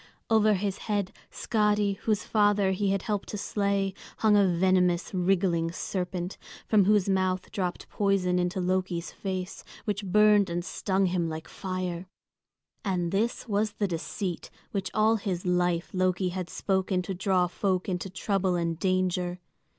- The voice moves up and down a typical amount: No, narrow, 2.0 semitones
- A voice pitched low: No, high, 190 Hz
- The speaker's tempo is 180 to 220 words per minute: No, average, 150 wpm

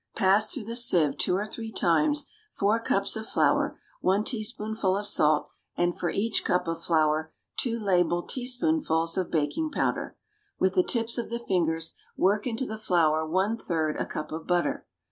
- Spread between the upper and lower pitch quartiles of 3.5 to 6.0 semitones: Yes, wide, 5.4 semitones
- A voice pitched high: Yes, high, 195 Hz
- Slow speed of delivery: No, average, 180 wpm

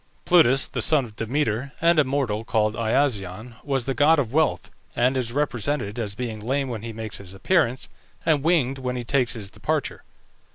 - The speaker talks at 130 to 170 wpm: No, average, 190 wpm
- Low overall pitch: Yes, low, 125 Hz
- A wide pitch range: No, average, 4.2 semitones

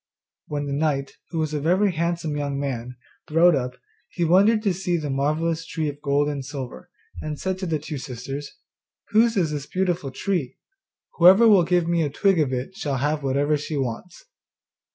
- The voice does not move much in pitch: No, average, 3.9 semitones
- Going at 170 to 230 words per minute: Yes, average, 190 wpm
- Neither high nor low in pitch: Yes, medium, 155 Hz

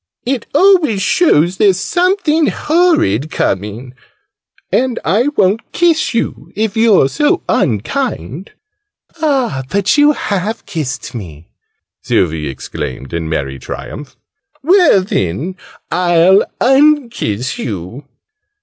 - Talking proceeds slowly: Yes, slow, 105 wpm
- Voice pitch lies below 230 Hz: Yes, high, 190 Hz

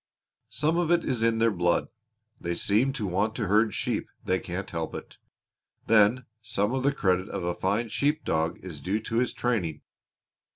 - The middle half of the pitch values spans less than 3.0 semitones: No, average, 4.9 semitones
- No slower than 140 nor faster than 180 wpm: No, average, 190 wpm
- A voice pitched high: No, low, 105 Hz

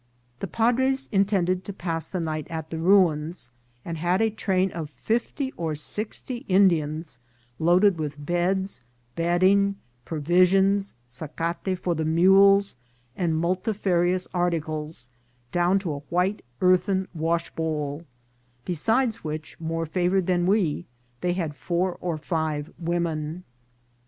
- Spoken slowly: Yes, slow, 120 wpm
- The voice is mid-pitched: Yes, medium, 175 Hz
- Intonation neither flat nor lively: Yes, average, 3.1 semitones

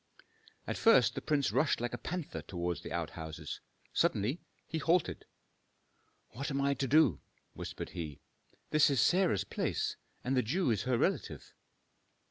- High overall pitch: No, low, 135 Hz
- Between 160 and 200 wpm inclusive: No, average, 150 wpm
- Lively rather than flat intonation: Yes, wide, 7.4 semitones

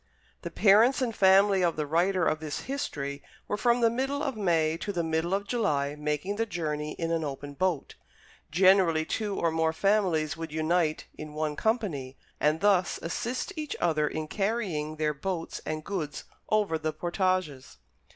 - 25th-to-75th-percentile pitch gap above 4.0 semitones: Yes, average, 4.7 semitones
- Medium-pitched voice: Yes, medium, 170 Hz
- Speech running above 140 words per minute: Yes, average, 170 wpm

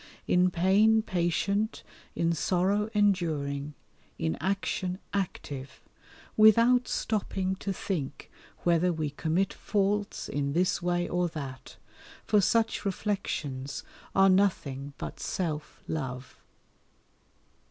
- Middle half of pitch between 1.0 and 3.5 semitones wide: No, average, 5.0 semitones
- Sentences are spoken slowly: Yes, slow, 100 wpm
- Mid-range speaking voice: Yes, medium, 180 Hz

